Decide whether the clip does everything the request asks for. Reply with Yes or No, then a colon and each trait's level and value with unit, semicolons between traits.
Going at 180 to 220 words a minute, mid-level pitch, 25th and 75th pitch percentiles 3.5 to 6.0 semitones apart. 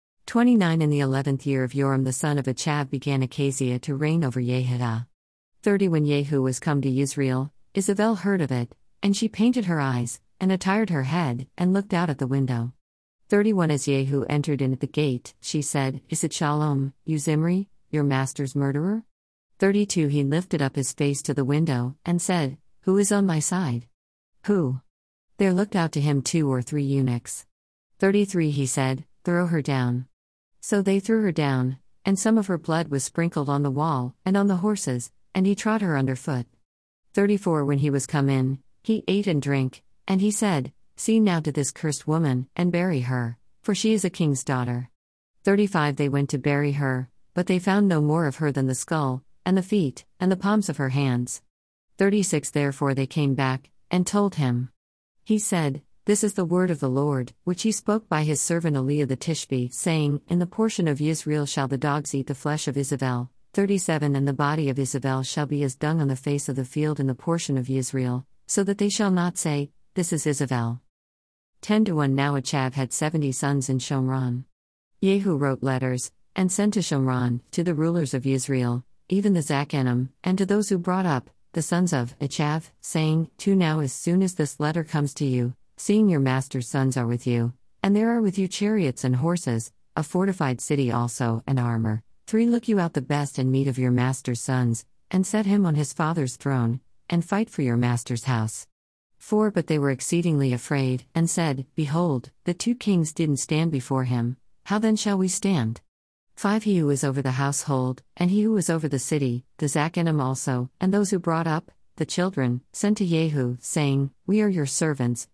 Yes: average, 200 wpm; medium, 145 Hz; average, 5.2 semitones